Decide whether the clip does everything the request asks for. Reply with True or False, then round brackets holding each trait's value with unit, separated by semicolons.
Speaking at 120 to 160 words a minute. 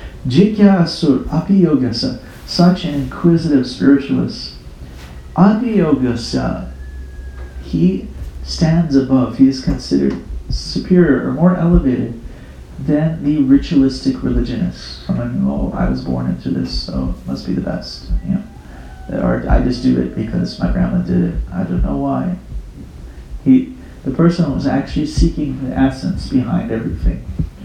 True (135 wpm)